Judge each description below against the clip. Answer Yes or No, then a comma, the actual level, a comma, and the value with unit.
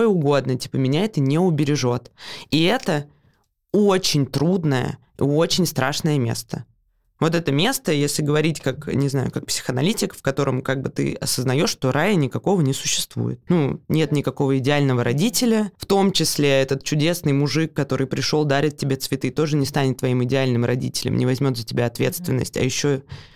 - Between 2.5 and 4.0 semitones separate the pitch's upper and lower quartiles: Yes, average, 3.2 semitones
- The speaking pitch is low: No, medium, 145 Hz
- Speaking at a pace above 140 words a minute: Yes, fast, 160 wpm